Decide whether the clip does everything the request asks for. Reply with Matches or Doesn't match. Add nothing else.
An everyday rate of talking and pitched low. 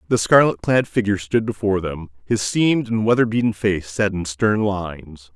Matches